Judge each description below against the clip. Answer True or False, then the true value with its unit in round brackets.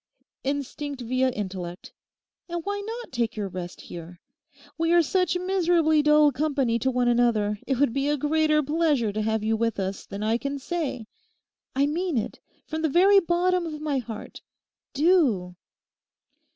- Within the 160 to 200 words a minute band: True (165 wpm)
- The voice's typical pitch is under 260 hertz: False (280 Hz)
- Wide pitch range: True (6.4 semitones)